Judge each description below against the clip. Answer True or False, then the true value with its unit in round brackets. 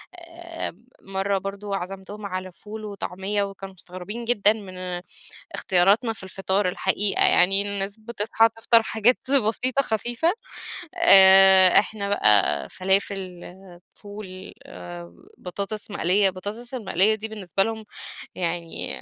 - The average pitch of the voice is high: True (200 Hz)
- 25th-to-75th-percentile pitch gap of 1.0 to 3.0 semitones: True (2.5 semitones)